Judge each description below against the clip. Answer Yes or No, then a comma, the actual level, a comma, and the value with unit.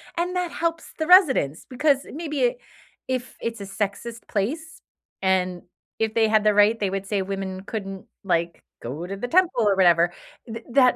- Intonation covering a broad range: Yes, wide, 6.3 semitones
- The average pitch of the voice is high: Yes, high, 215 Hz